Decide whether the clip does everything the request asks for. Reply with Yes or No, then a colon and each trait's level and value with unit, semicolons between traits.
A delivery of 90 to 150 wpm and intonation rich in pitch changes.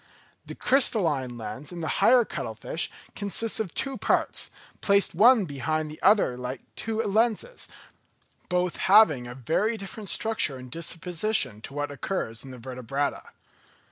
Yes: average, 145 wpm; wide, 8.3 semitones